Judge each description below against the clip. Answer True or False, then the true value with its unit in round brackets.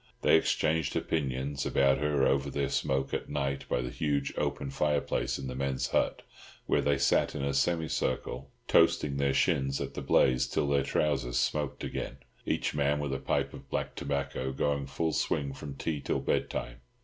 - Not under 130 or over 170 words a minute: False (180 wpm)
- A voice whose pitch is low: True (70 Hz)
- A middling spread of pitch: False (1.3 semitones)